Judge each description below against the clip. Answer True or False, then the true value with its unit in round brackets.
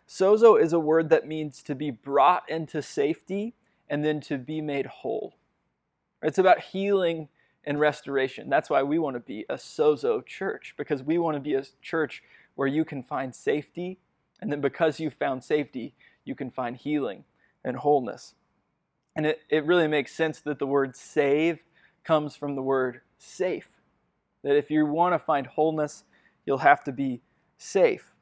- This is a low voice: False (150 Hz)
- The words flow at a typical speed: True (175 wpm)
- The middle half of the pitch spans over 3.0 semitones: False (2.6 semitones)